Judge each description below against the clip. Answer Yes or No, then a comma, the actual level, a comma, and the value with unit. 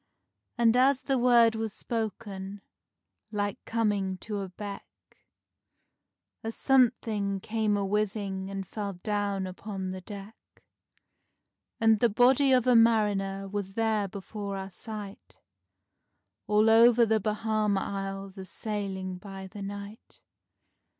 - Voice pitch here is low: No, high, 205 Hz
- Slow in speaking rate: Yes, slow, 120 wpm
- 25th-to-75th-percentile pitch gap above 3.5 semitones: No, narrow, 2.4 semitones